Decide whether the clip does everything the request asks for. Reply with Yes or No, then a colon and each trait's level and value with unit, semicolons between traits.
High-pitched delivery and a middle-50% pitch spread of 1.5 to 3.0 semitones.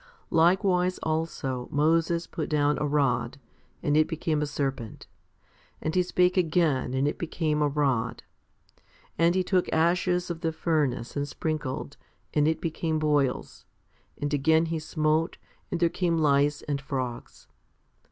No: medium, 155 Hz; narrow, 2.6 semitones